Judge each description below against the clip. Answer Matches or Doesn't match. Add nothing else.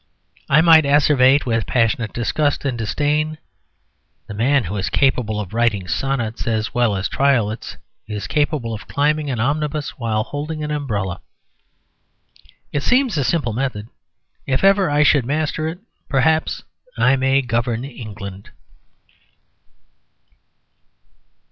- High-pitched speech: Doesn't match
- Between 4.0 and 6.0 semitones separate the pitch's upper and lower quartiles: Matches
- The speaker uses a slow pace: Matches